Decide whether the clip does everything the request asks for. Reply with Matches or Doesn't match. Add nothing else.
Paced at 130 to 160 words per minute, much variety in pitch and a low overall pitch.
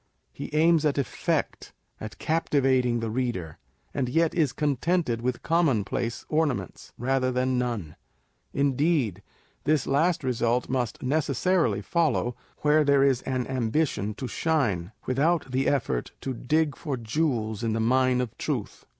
Doesn't match